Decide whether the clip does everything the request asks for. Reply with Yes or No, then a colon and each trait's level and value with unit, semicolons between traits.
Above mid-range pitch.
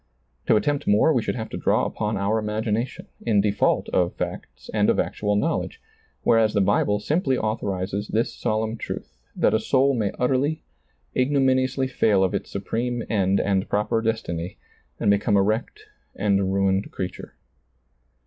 No: low, 110 Hz